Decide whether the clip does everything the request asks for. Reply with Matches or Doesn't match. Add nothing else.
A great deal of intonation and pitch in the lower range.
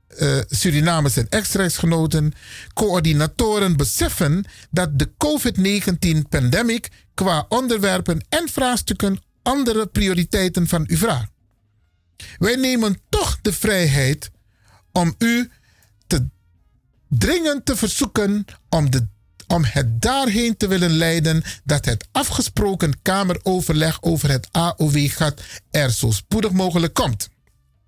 Doesn't match